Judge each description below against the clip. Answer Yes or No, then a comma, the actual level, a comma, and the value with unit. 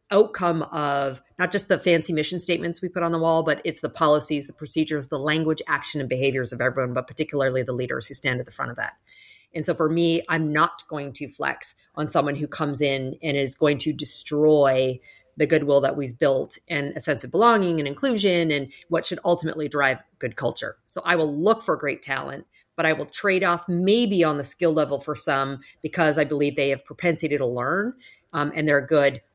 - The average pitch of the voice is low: No, medium, 150 Hz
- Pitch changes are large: No, average, 3.2 semitones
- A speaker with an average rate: No, fast, 215 wpm